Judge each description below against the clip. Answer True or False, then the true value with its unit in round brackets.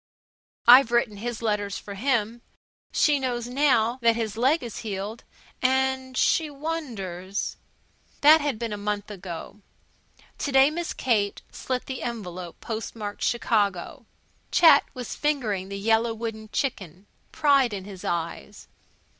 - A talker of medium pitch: False (230 Hz)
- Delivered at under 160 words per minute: True (140 wpm)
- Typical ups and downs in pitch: True (4.4 semitones)